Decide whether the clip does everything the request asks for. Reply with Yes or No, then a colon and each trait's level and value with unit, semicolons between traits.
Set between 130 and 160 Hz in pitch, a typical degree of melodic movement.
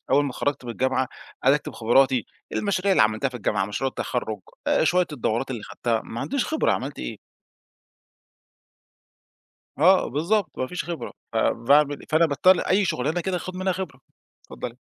No: medium, 140 Hz; wide, 6.7 semitones